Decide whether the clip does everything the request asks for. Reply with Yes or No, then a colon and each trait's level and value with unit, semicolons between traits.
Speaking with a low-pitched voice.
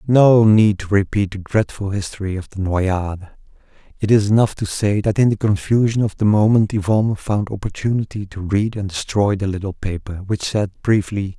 Yes: low, 100 Hz